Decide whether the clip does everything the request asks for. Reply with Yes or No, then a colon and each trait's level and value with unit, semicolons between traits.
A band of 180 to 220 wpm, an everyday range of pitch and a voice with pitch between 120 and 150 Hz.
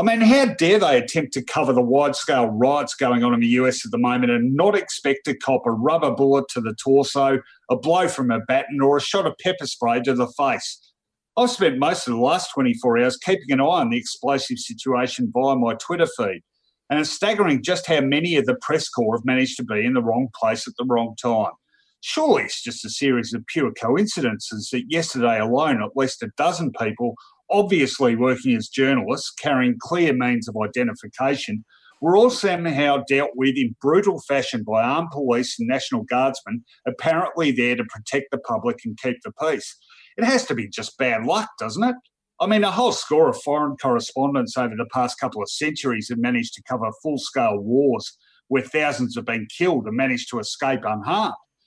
No: average, 200 wpm; wide, 6.4 semitones; low, 135 Hz